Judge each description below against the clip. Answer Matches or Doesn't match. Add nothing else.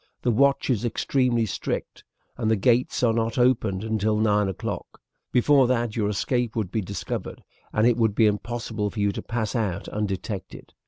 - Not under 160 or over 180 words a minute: Matches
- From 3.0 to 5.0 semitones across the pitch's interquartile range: Doesn't match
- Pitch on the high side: Doesn't match